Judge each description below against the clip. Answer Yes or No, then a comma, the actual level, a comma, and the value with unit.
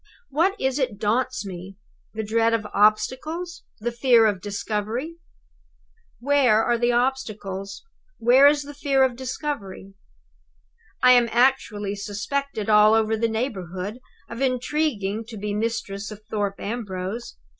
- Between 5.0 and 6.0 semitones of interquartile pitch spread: No, average, 4.1 semitones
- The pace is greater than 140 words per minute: No, slow, 135 wpm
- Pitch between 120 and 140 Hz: No, high, 230 Hz